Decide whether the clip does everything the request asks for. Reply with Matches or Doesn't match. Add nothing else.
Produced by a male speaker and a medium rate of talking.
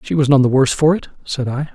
Doesn't match